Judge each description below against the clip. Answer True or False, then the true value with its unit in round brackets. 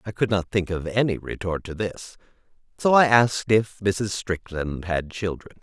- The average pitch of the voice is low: True (100 Hz)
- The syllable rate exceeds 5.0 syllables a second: False (4.6 syllables/s)